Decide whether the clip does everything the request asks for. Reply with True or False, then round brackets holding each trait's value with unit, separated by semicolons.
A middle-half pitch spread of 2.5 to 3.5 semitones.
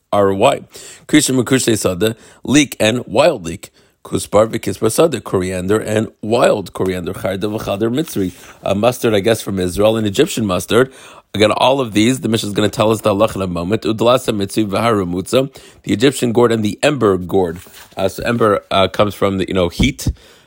True (2.8 semitones)